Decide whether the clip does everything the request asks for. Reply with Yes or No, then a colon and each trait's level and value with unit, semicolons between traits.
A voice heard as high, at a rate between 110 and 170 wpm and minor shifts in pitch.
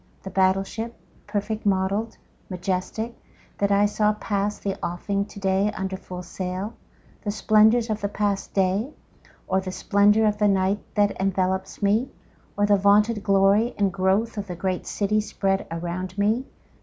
Yes: high, 200 Hz; average, 155 wpm; narrow, 1.8 semitones